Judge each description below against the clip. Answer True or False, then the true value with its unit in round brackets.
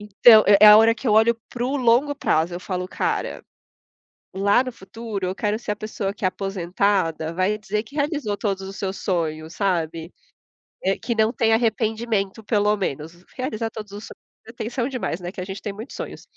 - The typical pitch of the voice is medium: False (210 Hz)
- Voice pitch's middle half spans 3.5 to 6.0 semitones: False (3.1 semitones)